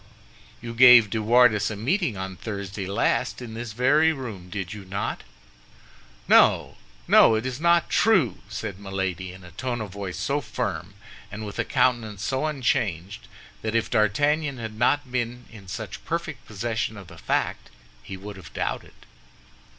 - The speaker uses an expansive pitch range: No, average, 4.1 semitones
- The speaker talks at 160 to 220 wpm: Yes, average, 165 wpm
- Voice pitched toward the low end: Yes, low, 110 Hz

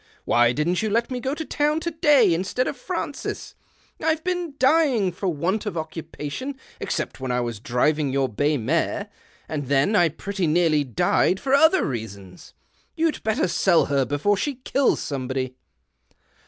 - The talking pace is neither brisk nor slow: Yes, average, 165 wpm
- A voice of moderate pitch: Yes, medium, 175 Hz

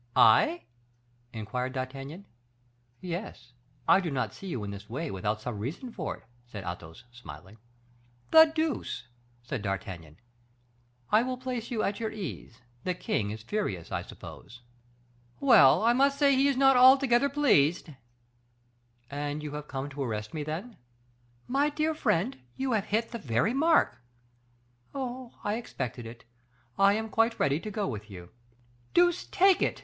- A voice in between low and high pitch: Yes, medium, 175 Hz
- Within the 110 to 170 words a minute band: Yes, average, 155 wpm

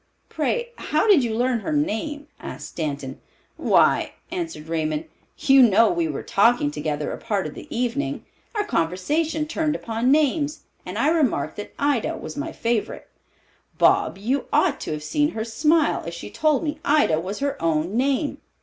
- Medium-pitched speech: No, high, 245 Hz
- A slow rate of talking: No, average, 170 wpm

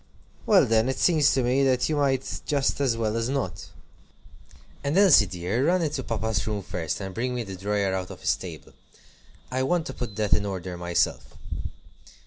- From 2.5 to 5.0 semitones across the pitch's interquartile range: No, wide, 5.5 semitones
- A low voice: Yes, low, 115 Hz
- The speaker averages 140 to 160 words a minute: No, average, 190 wpm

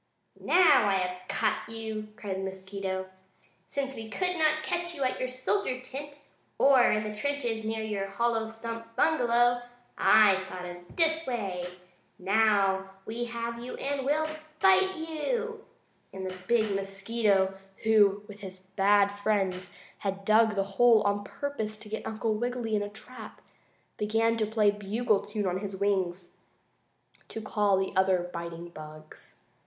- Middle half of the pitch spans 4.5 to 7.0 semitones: No, average, 3.8 semitones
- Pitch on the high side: Yes, high, 215 Hz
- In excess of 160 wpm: No, average, 155 wpm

